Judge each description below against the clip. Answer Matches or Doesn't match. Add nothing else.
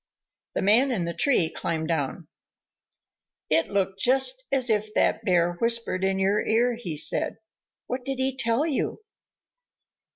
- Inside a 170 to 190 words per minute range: Doesn't match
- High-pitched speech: Matches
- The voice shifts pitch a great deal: Matches